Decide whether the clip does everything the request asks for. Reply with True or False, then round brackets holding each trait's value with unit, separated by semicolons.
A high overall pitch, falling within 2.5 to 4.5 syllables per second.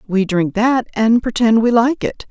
True (225 Hz; 4.3 syllables/s)